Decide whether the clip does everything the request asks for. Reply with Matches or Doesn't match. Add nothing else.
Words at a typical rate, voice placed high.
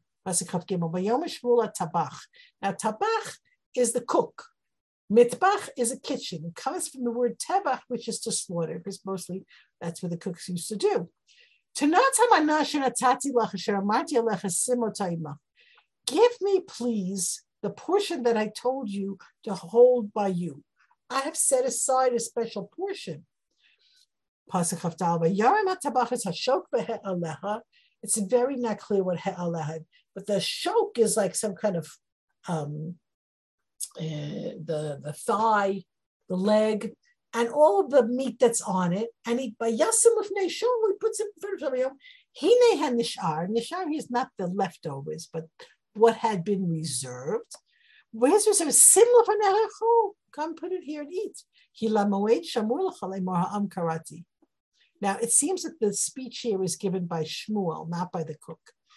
Doesn't match